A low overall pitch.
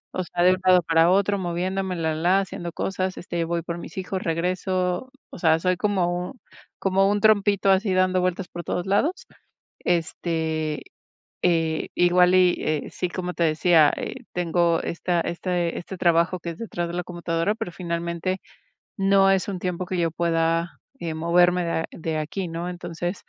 No: medium, 175 Hz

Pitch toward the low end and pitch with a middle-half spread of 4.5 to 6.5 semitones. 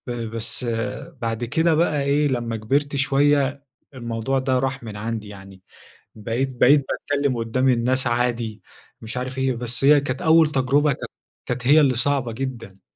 No: low, 130 Hz; average, 3.3 semitones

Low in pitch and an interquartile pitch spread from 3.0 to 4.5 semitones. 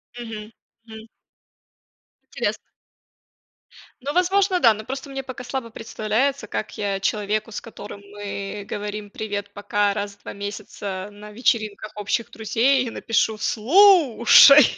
No: high, 220 Hz; average, 3.6 semitones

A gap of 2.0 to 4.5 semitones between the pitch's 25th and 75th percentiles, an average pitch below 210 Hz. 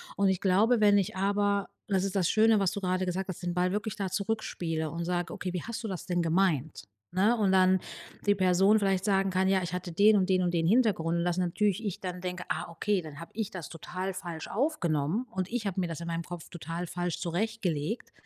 Yes: narrow, 2.6 semitones; medium, 185 Hz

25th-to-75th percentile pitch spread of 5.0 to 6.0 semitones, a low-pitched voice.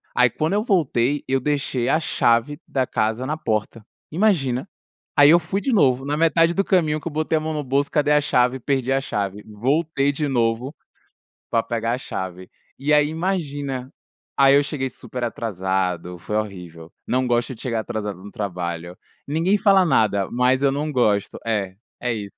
Yes: wide, 5.4 semitones; low, 130 Hz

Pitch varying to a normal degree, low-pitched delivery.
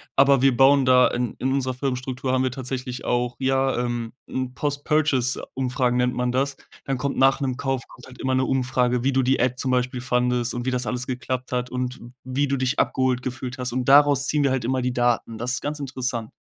No: narrow, 1.2 semitones; low, 130 Hz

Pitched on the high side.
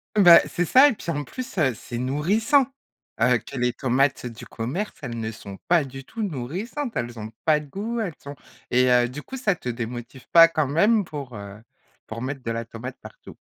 No: medium, 140 Hz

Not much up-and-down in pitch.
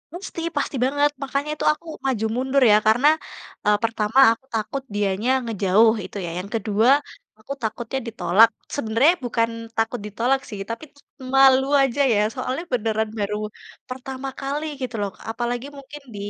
No: average, 3.8 semitones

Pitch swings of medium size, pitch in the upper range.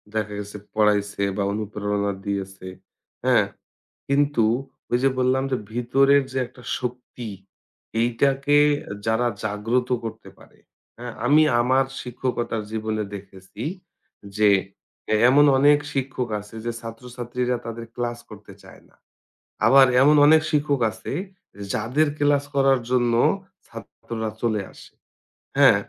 No: average, 3.7 semitones; low, 120 Hz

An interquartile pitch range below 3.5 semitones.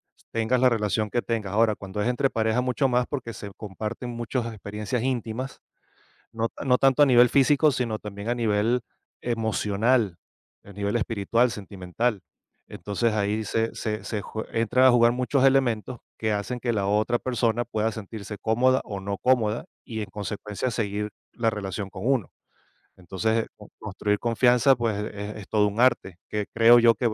Yes: average, 2.7 semitones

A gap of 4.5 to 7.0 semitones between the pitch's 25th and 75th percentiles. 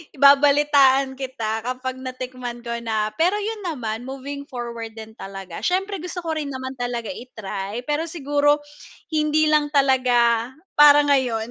No: average, 3.8 semitones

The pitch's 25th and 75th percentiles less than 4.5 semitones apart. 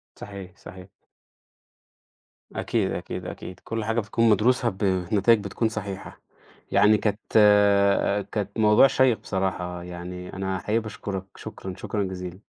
Yes: narrow, 2.6 semitones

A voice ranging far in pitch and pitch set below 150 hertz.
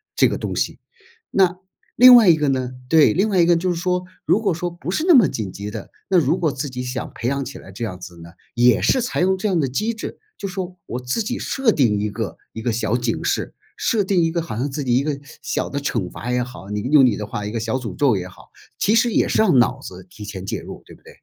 Yes: wide, 8.1 semitones; medium, 140 Hz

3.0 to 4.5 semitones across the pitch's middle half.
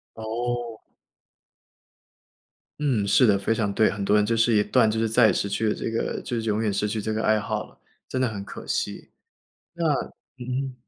No: narrow, 2.4 semitones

